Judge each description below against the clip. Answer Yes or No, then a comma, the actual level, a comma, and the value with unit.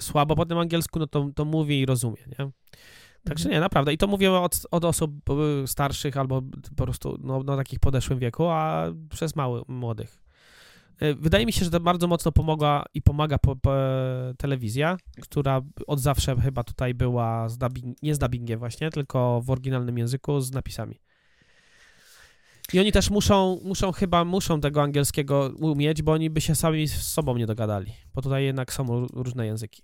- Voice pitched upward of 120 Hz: Yes, medium, 140 Hz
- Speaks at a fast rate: Yes, fast, 180 wpm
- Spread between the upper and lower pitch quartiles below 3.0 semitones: No, average, 3.9 semitones